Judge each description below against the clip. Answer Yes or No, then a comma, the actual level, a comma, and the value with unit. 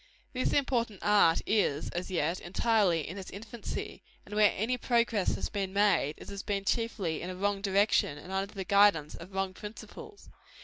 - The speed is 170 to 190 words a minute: Yes, average, 180 wpm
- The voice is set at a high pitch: Yes, high, 200 Hz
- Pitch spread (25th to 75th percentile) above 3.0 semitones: No, average, 2.7 semitones